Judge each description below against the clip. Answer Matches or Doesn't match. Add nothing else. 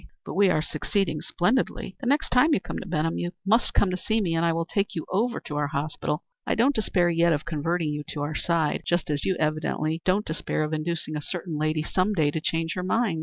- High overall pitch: Doesn't match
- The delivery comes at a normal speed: Doesn't match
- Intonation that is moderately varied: Matches